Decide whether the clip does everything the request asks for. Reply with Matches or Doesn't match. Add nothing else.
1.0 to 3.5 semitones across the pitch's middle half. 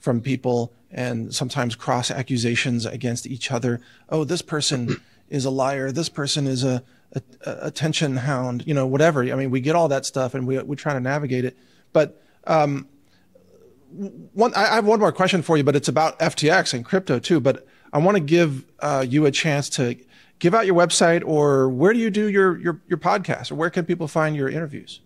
Doesn't match